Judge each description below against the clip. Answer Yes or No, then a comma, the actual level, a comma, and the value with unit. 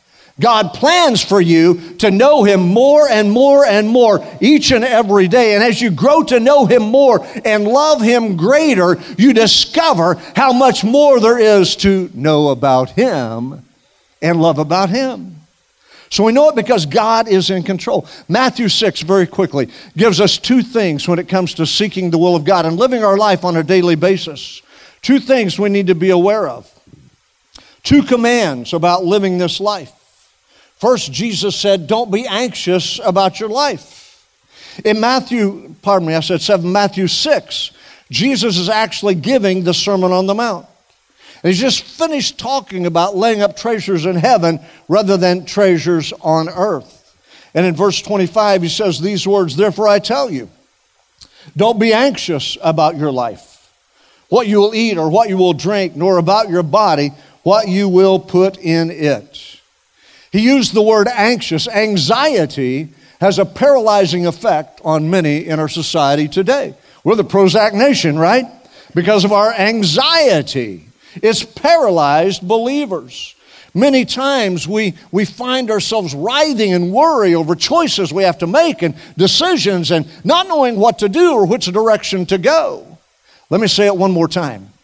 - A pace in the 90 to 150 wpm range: No, average, 165 wpm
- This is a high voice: Yes, high, 200 Hz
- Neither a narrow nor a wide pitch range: Yes, average, 4.8 semitones